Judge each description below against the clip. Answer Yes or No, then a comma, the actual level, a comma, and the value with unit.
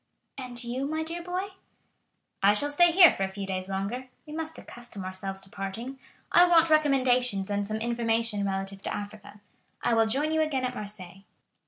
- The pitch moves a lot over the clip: Yes, wide, 6.7 semitones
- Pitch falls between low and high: No, high, 235 Hz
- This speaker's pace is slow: No, average, 185 wpm